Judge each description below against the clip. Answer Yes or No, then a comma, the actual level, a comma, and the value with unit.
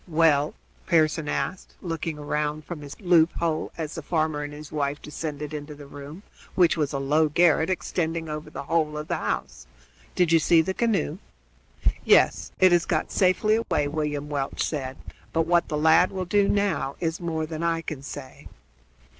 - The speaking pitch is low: No, medium, 155 Hz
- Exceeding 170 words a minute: Yes, average, 180 wpm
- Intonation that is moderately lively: No, narrow, 2.3 semitones